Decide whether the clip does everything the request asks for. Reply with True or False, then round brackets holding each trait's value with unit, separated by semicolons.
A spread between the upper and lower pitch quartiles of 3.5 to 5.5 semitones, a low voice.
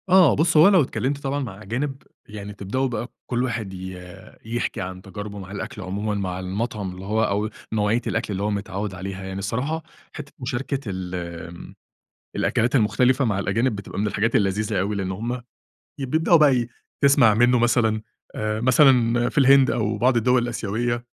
True (4.1 semitones; 110 Hz)